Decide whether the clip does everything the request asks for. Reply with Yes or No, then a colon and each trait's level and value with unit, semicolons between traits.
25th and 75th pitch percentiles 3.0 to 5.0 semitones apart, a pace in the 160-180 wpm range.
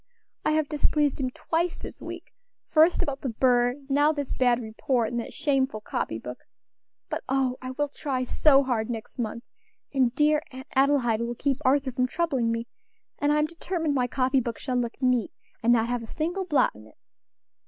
No: average, 3.3 semitones; average, 195 wpm